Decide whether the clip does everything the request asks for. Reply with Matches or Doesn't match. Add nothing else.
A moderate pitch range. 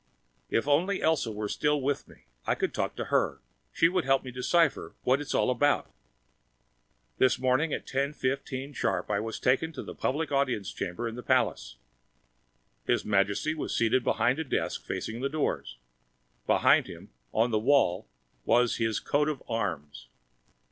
Matches